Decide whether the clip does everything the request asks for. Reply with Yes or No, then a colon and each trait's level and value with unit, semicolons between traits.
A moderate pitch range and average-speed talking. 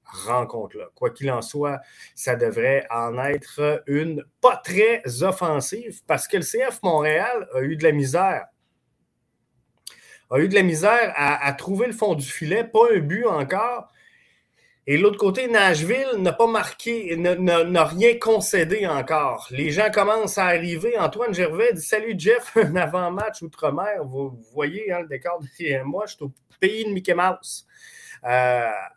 No: wide, 7.1 semitones; average, 165 wpm